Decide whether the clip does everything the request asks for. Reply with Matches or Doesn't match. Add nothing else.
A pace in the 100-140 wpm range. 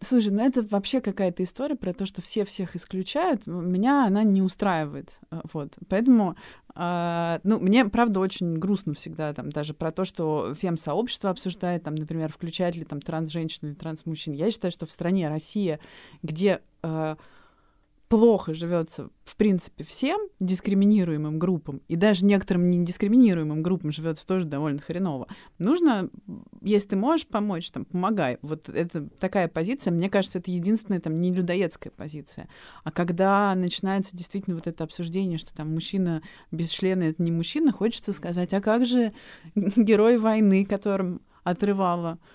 Doesn't match